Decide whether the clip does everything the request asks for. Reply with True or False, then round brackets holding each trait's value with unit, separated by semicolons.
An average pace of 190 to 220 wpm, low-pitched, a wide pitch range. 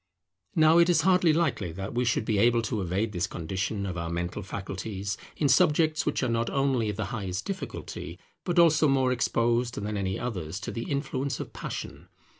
True (195 wpm; 115 Hz; 6.3 semitones)